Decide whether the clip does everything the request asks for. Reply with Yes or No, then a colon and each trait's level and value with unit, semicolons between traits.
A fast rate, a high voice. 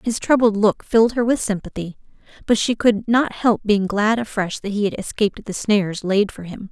Yes: fast, 215 wpm; high, 210 Hz